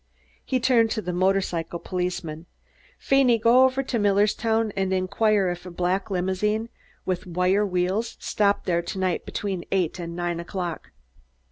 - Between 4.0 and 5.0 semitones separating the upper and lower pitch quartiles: No, average, 3.4 semitones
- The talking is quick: No, average, 150 wpm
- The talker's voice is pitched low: No, high, 190 Hz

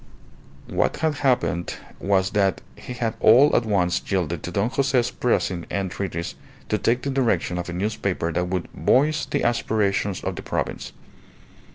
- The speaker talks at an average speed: Yes, average, 165 wpm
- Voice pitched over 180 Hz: No, low, 100 Hz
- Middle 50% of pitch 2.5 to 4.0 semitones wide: No, wide, 5.4 semitones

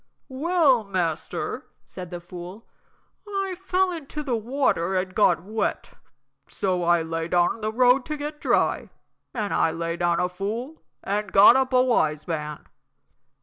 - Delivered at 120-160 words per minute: Yes, average, 155 wpm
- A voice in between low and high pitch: No, high, 205 Hz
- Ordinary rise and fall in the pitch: No, wide, 7.2 semitones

